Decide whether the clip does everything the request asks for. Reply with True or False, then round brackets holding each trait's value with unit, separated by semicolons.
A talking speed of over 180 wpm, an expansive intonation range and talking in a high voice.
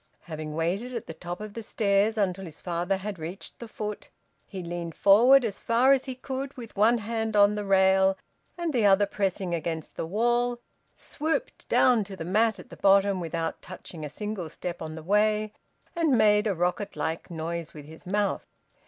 False (195 wpm; 4.3 semitones; 200 Hz)